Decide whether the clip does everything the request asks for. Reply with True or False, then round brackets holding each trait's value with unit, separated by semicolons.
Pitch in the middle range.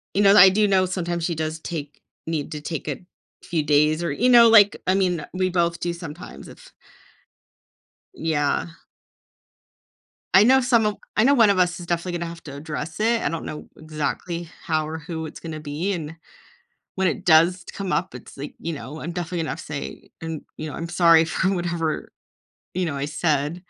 True (170 Hz)